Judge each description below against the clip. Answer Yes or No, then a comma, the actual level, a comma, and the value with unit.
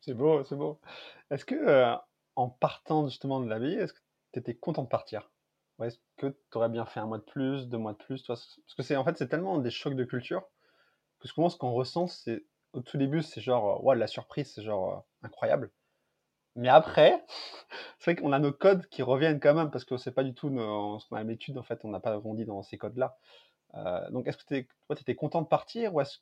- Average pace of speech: No, fast, 245 wpm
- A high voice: No, low, 130 Hz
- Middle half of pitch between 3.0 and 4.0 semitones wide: No, average, 4.7 semitones